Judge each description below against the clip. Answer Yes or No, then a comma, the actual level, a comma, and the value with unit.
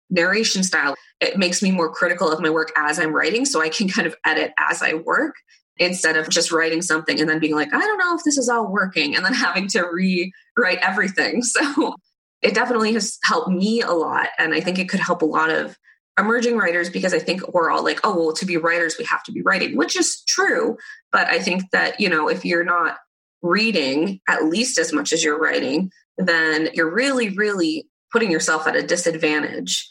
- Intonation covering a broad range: Yes, wide, 6.0 semitones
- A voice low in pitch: No, medium, 175 Hz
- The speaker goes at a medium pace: No, fast, 220 wpm